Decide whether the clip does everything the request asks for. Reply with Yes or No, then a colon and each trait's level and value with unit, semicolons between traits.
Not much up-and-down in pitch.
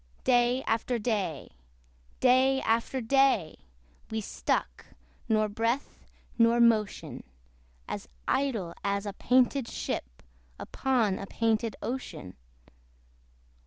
No: average, 3.4 semitones